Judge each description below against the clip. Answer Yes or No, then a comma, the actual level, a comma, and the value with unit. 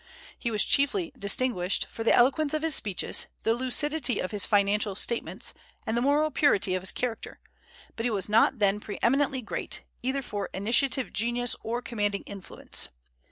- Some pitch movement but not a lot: Yes, average, 4.6 semitones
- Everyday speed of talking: Yes, average, 170 wpm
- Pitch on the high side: Yes, high, 235 Hz